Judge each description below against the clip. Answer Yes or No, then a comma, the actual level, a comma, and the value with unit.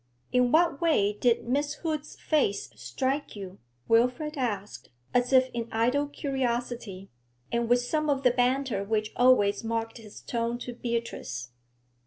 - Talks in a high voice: Yes, high, 245 Hz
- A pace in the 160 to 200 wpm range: No, average, 145 wpm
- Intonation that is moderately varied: Yes, average, 3.3 semitones